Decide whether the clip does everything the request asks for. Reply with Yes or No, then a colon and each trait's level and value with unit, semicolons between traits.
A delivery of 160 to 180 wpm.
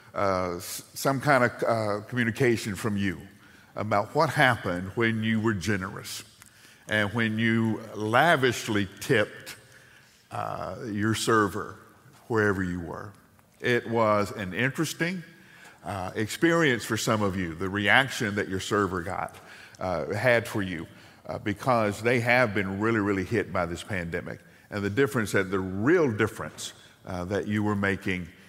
No: average, 145 wpm